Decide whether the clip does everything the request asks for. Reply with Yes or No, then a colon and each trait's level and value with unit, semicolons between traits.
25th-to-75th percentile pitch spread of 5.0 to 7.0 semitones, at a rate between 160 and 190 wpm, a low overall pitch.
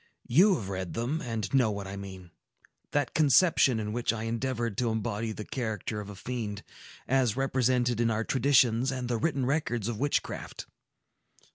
No: average, 3.4 semitones; average, 165 wpm; low, 120 Hz